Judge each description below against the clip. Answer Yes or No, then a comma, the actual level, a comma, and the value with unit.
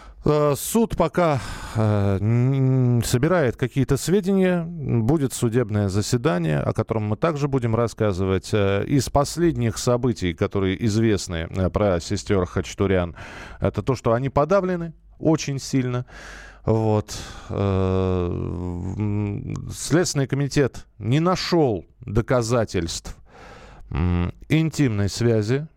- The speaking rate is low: Yes, slow, 85 wpm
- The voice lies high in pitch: No, low, 120 Hz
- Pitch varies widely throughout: Yes, wide, 6.0 semitones